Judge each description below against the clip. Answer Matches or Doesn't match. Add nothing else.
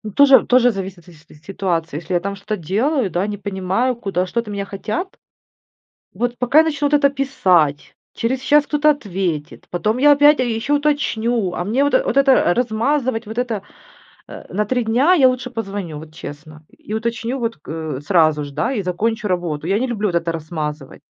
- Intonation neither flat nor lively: Doesn't match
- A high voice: Matches